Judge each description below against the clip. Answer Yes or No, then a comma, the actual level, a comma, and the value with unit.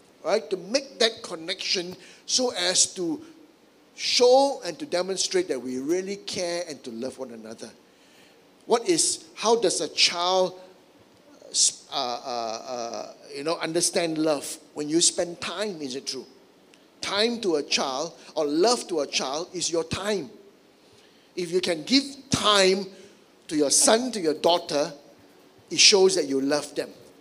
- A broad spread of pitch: Yes, wide, 5.8 semitones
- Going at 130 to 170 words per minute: Yes, average, 155 wpm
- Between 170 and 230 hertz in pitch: Yes, medium, 185 Hz